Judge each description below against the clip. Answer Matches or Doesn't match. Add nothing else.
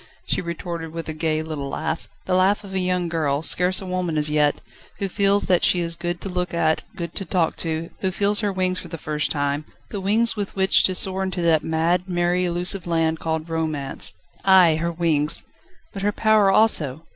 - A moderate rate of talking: Doesn't match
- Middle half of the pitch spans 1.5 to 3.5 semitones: Matches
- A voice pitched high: Doesn't match